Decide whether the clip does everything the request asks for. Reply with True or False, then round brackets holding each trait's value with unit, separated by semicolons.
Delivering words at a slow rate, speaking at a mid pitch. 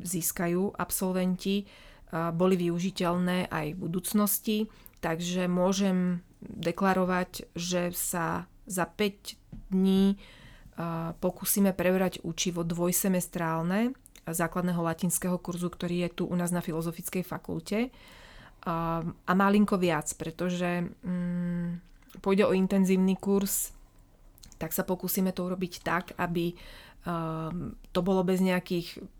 True (100 wpm; 180 Hz)